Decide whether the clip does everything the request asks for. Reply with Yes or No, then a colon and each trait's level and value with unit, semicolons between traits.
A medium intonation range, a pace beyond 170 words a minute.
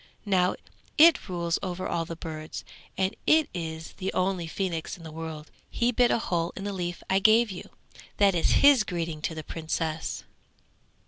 Yes: average, 3.4 semitones; average, 180 wpm